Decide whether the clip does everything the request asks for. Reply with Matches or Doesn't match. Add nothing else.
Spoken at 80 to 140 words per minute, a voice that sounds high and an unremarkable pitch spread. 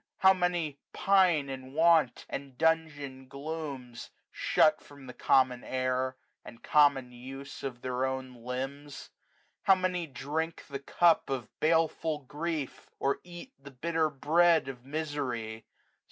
Doesn't match